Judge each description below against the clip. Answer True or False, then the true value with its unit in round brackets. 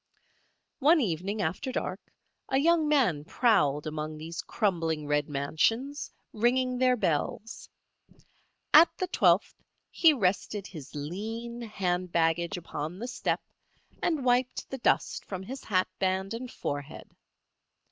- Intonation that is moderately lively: False (7.5 semitones)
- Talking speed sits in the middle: False (125 wpm)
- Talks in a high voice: True (195 Hz)